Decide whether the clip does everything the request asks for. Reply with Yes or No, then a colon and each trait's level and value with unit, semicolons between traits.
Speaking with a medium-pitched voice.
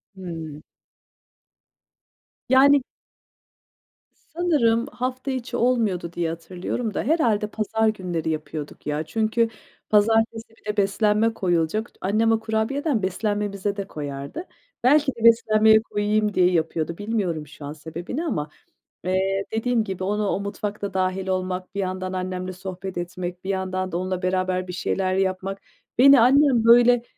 No: high, 200 Hz